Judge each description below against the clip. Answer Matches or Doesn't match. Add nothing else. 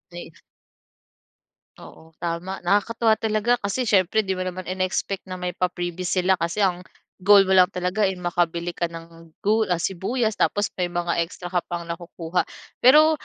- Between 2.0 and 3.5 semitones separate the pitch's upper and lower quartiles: Matches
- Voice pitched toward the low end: Doesn't match